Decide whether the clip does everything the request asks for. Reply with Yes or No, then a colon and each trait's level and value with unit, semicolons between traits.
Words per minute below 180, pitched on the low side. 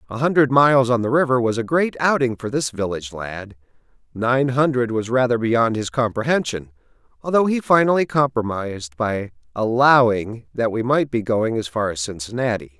Yes: average, 170 wpm; low, 120 Hz